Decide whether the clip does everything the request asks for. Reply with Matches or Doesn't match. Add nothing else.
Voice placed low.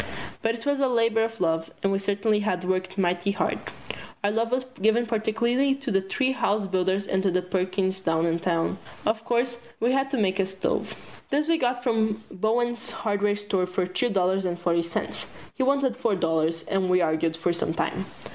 Doesn't match